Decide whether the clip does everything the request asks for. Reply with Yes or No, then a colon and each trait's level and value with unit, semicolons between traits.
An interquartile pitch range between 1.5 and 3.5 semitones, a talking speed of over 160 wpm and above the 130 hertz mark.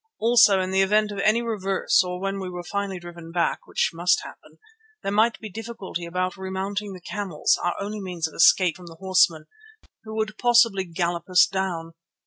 Yes: average, 2.9 semitones; average, 190 wpm; high, 190 Hz